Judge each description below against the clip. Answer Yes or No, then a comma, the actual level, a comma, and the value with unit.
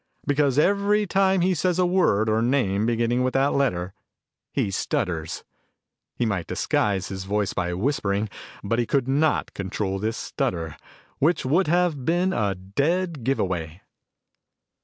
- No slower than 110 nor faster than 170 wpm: Yes, average, 150 wpm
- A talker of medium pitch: No, low, 120 Hz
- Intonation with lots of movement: Yes, wide, 8.5 semitones